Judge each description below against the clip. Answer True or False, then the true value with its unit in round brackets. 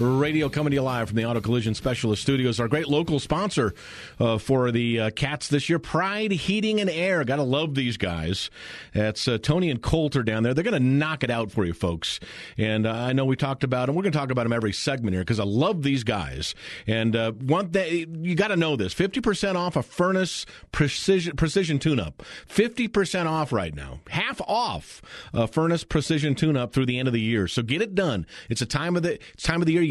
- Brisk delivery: True (235 wpm)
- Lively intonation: True (5.9 semitones)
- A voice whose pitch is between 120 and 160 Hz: True (140 Hz)